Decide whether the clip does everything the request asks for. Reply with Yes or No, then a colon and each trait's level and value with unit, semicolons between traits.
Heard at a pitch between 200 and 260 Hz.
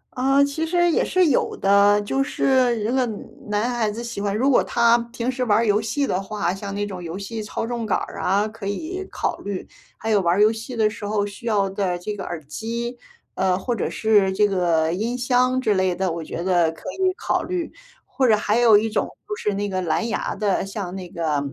Yes: high, 210 Hz